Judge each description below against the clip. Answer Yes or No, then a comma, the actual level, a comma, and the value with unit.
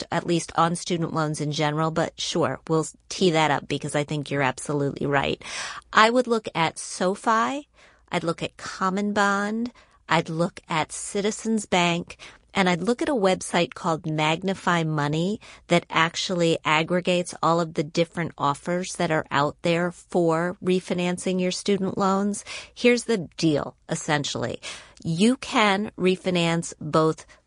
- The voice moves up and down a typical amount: Yes, average, 3.4 semitones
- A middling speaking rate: Yes, average, 150 wpm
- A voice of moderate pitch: Yes, medium, 175 Hz